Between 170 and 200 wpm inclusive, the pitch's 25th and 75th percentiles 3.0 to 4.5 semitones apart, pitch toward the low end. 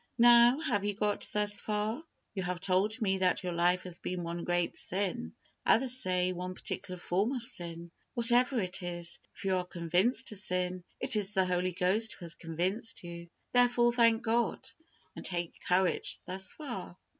No: average, 180 wpm; average, 4.1 semitones; high, 190 Hz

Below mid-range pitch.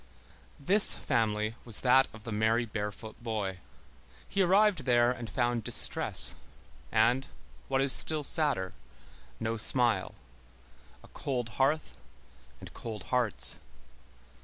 Yes: low, 120 Hz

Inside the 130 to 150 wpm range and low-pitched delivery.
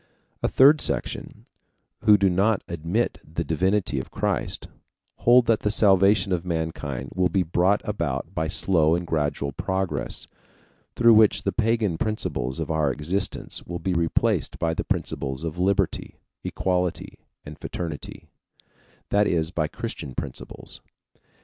Yes: average, 140 wpm; very low, 90 Hz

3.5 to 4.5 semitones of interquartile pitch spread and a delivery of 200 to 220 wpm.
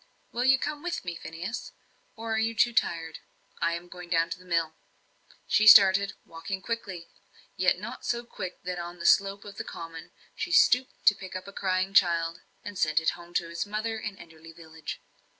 Yes: average, 4.1 semitones; fast, 205 wpm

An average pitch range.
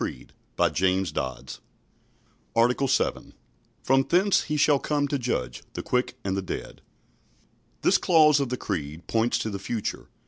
No: wide, 7.0 semitones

